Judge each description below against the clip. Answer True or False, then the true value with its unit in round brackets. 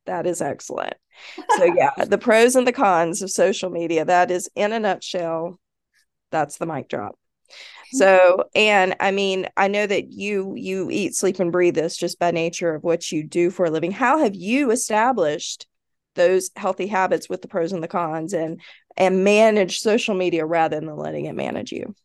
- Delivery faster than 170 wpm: True (190 wpm)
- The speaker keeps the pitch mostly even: False (3.0 semitones)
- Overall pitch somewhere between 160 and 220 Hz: True (185 Hz)